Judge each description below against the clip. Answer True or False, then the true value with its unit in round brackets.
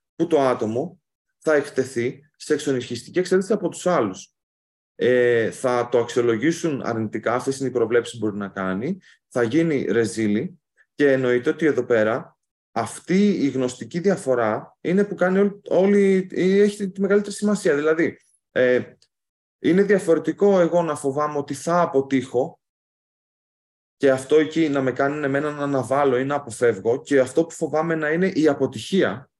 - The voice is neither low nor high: True (145 Hz)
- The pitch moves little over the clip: False (5.6 semitones)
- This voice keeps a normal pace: True (155 wpm)